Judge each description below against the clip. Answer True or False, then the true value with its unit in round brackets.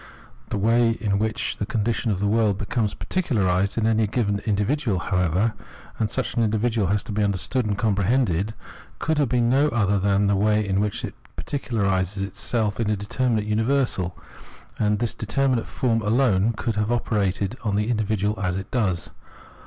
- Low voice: True (105 Hz)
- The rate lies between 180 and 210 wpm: True (190 wpm)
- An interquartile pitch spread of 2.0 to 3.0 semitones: True (2.7 semitones)